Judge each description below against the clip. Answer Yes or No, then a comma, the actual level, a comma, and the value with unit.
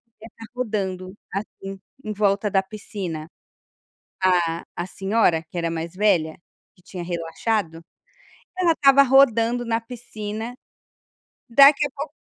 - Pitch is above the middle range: Yes, high, 205 Hz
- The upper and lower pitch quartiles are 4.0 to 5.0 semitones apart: Yes, average, 4.5 semitones